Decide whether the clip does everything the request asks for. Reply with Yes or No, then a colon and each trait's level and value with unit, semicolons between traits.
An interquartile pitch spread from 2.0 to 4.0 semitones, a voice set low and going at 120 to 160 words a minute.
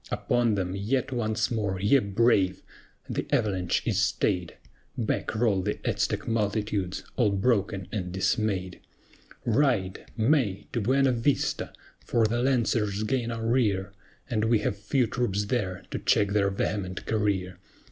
Yes: average, 3.4 semitones; low, 105 Hz; average, 140 wpm